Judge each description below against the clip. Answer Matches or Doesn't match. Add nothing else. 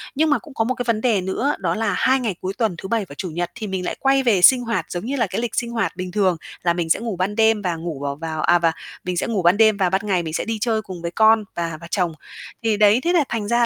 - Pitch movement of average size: Matches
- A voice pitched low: Doesn't match